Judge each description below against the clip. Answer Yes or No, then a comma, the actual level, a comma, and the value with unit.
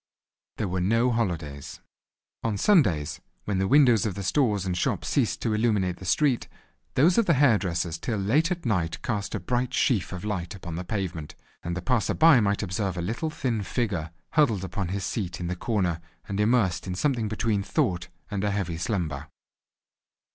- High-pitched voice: No, low, 100 Hz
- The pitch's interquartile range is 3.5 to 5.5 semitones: Yes, average, 4.7 semitones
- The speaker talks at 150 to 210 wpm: Yes, average, 190 wpm